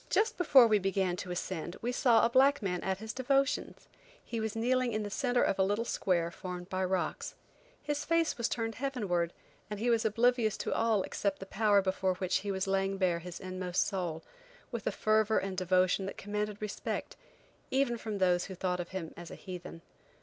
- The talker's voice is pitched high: Yes, high, 200 Hz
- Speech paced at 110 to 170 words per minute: No, fast, 205 wpm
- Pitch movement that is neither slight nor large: Yes, average, 3.8 semitones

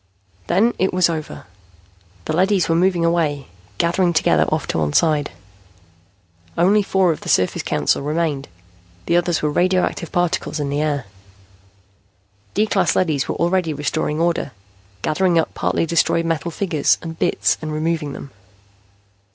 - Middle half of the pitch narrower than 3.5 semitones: Yes, narrow, 2.6 semitones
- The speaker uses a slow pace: No, average, 150 wpm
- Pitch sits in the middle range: Yes, medium, 165 Hz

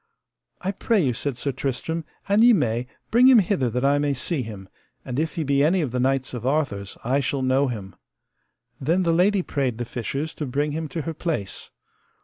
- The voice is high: No, medium, 140 Hz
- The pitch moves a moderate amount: Yes, average, 4.8 semitones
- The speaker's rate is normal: No, fast, 210 wpm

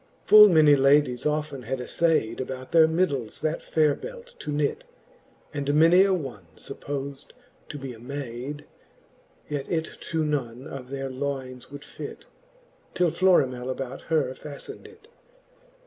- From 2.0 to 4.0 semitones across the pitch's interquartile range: Yes, average, 3.4 semitones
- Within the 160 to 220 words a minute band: No, average, 150 wpm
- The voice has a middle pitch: Yes, medium, 145 Hz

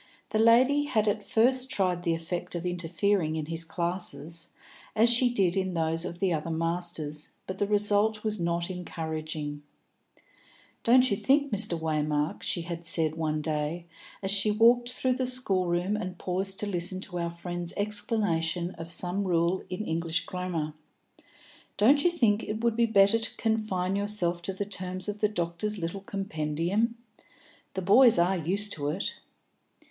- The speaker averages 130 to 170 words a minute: Yes, average, 165 wpm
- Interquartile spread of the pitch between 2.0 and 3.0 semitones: No, average, 4.0 semitones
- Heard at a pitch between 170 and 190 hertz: Yes, medium, 185 Hz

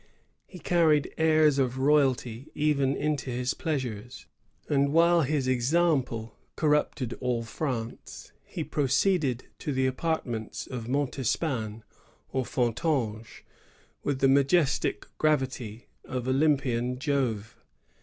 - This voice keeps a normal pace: No, slow, 105 wpm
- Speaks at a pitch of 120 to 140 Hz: Yes, low, 135 Hz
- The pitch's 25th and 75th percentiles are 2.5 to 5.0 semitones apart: Yes, average, 3.7 semitones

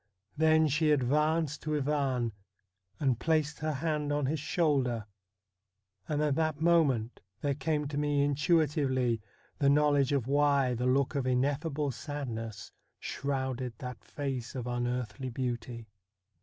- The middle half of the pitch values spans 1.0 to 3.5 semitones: Yes, average, 3.0 semitones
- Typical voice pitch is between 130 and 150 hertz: Yes, medium, 140 Hz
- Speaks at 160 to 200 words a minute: No, slow, 135 wpm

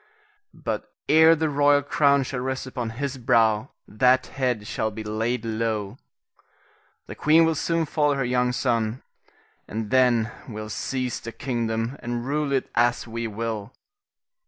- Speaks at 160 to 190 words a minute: No, average, 150 wpm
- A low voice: Yes, low, 125 Hz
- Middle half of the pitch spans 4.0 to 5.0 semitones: No, average, 3.6 semitones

